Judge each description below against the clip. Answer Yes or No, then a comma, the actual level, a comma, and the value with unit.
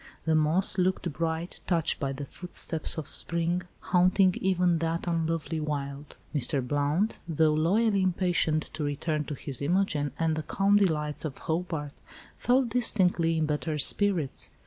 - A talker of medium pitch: Yes, medium, 165 Hz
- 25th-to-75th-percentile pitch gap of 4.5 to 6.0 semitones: No, average, 3.1 semitones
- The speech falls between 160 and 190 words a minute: No, average, 145 wpm